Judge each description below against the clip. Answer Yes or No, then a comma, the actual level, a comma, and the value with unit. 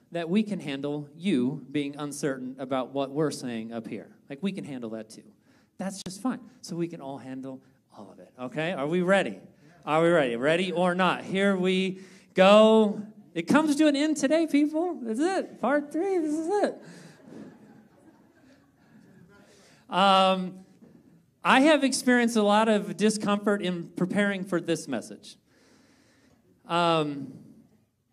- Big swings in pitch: Yes, wide, 6.4 semitones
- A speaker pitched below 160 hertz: No, medium, 185 Hz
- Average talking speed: Yes, average, 150 wpm